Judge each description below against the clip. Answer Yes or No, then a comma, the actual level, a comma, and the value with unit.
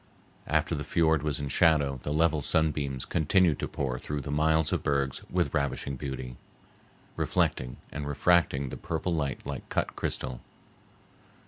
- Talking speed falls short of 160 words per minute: Yes, average, 150 wpm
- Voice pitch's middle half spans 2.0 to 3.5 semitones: Yes, narrow, 2.6 semitones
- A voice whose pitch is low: Yes, very low, 75 Hz